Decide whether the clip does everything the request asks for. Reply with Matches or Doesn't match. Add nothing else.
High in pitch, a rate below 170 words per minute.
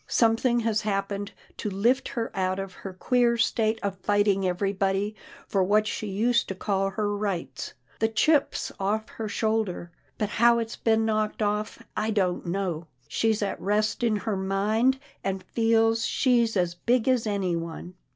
Matches